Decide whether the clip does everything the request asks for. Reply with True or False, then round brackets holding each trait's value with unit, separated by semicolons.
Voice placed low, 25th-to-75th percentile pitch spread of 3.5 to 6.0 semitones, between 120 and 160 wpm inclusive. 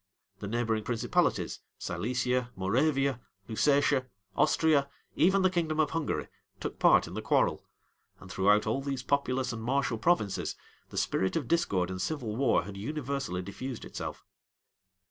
True (125 Hz; 4.8 semitones; 145 wpm)